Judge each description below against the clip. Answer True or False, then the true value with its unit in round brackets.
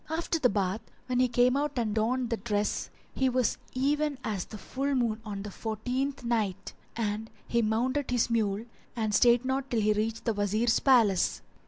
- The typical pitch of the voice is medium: False (235 Hz)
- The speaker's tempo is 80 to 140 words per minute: False (185 wpm)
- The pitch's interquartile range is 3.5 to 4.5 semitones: False (3.1 semitones)